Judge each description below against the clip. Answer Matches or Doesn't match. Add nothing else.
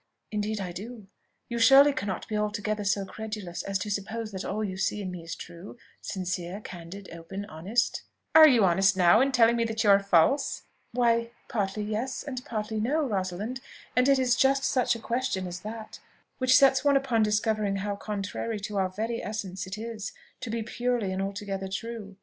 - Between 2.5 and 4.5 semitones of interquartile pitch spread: Matches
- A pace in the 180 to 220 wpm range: Matches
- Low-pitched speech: Doesn't match